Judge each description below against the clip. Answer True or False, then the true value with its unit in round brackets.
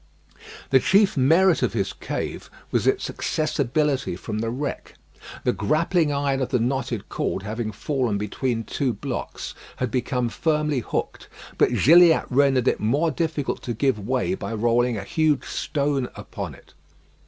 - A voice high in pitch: False (135 Hz)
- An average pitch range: True (4.4 semitones)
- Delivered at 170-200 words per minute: False (155 wpm)